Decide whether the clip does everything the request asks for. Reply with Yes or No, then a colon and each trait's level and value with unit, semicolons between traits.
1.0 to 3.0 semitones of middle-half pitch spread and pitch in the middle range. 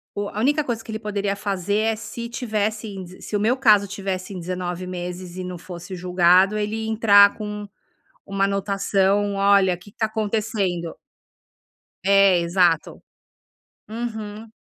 No: narrow, 2.6 semitones; high, 200 Hz